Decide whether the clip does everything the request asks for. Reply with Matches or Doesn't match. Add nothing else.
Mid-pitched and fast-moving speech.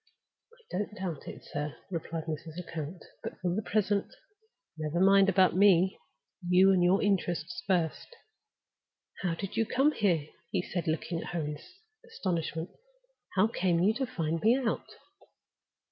Doesn't match